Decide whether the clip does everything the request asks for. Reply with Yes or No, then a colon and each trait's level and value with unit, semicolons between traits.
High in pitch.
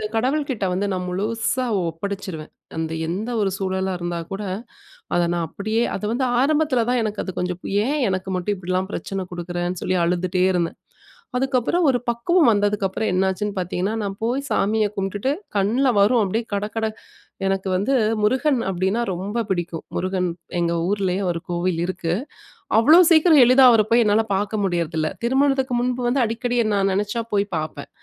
Yes: high, 200 Hz